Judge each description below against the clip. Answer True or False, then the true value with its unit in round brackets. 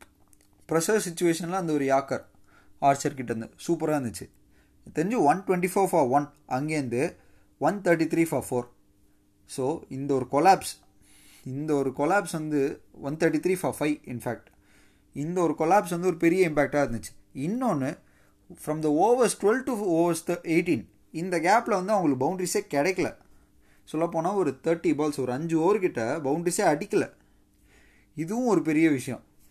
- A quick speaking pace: True (140 wpm)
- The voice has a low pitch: False (150 Hz)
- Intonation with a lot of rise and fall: True (5.8 semitones)